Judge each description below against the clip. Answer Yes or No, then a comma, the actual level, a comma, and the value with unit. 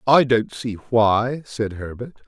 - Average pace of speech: Yes, average, 160 wpm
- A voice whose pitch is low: Yes, low, 115 Hz